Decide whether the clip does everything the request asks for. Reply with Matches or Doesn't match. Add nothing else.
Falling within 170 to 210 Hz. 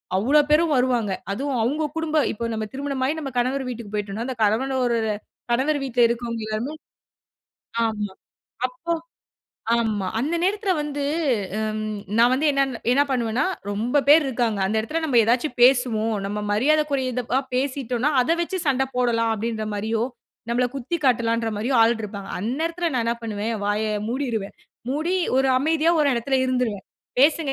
Doesn't match